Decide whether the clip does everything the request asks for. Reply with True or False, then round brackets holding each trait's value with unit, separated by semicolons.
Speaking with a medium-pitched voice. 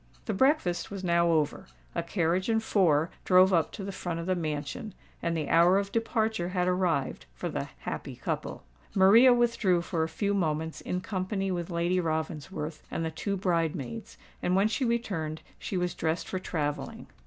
True (180 Hz)